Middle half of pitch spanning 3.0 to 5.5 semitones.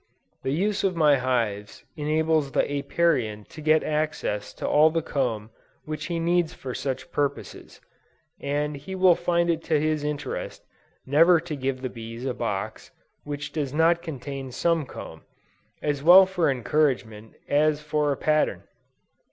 Yes: average, 3.5 semitones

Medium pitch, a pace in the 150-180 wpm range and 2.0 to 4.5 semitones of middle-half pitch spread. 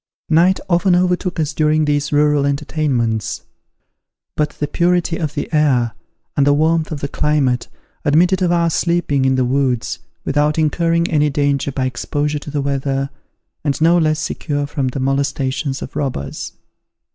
Yes: medium, 150 Hz; average, 160 wpm; average, 2.7 semitones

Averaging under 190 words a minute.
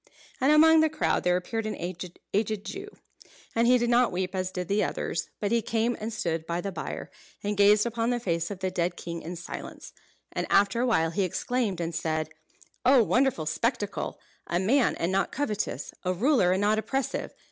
No: average, 200 wpm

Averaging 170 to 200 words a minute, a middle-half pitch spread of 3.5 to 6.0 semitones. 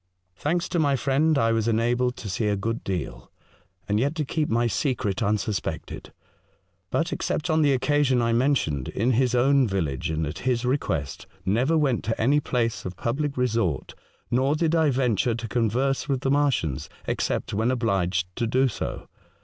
Yes: average, 180 wpm; average, 4.5 semitones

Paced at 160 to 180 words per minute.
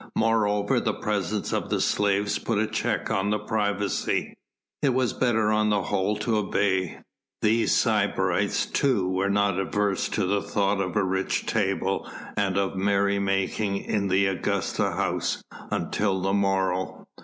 No: average, 150 wpm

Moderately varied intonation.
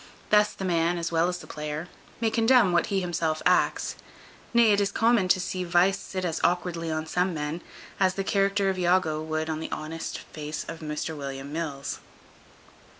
Yes: average, 3.5 semitones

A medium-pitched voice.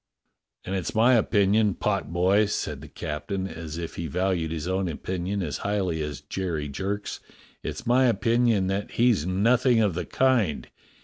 No: very low, 95 Hz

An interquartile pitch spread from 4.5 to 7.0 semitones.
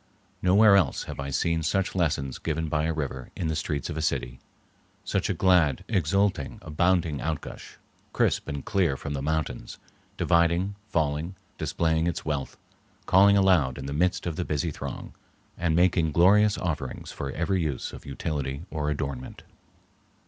No: average, 3.9 semitones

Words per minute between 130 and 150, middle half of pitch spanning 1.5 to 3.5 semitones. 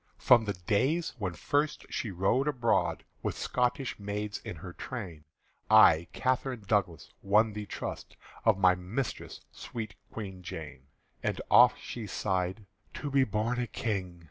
No: average, 145 wpm; average, 4.8 semitones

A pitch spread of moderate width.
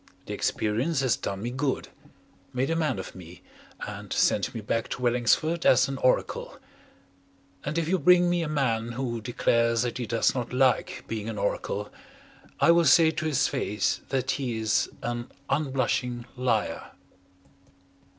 Yes: average, 4.1 semitones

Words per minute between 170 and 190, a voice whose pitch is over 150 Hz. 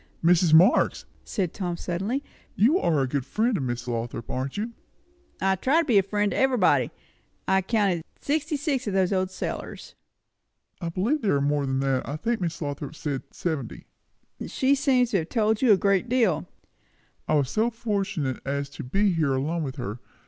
Yes: average, 185 wpm; medium, 185 Hz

